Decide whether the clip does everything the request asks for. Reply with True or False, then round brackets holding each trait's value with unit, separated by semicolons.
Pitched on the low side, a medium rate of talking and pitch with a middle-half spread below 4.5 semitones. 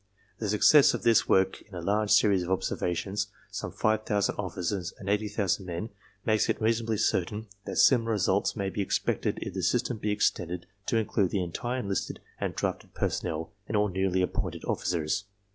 True (100 Hz; 180 wpm; 2.8 semitones)